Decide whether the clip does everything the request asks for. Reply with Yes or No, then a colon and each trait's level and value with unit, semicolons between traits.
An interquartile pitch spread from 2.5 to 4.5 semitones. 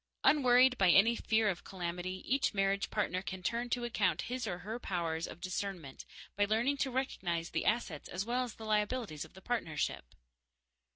No: average, 5.1 semitones